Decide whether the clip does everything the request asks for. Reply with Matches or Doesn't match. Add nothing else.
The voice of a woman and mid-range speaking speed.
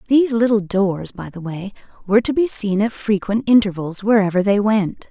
Matches